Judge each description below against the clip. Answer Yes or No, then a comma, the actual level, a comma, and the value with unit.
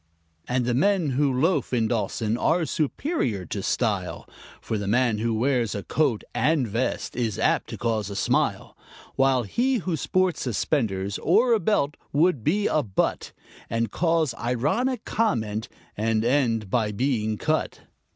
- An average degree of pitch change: No, wide, 6.1 semitones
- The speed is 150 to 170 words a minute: Yes, average, 155 wpm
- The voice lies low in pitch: Yes, low, 125 Hz